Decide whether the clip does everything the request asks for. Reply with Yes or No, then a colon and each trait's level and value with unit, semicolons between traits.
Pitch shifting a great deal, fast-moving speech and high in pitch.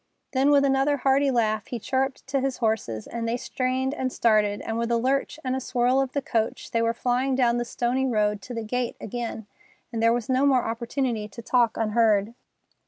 No: narrow, 2.6 semitones; fast, 210 wpm; high, 240 Hz